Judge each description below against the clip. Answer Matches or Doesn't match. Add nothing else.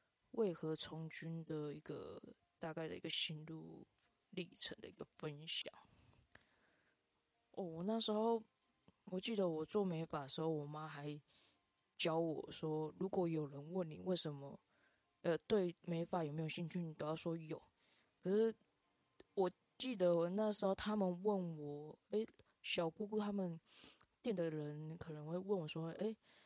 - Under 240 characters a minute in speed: Matches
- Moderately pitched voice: Matches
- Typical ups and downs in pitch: Matches